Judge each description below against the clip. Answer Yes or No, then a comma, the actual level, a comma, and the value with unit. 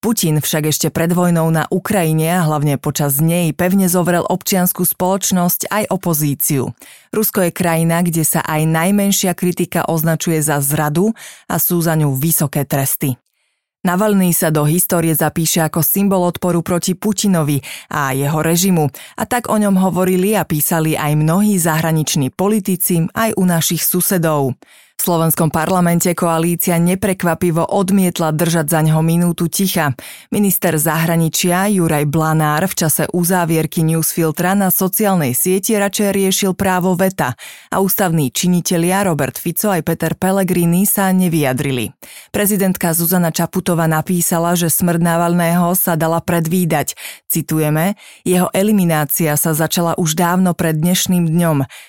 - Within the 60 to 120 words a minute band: No, average, 135 wpm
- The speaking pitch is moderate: Yes, medium, 170 Hz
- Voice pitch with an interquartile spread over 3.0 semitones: No, average, 2.7 semitones